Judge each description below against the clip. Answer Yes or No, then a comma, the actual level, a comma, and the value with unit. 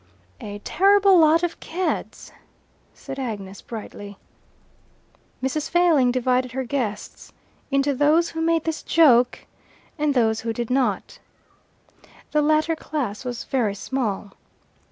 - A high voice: Yes, very high, 265 Hz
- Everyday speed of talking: No, slow, 120 wpm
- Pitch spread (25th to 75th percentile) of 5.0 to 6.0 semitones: Yes, wide, 5.4 semitones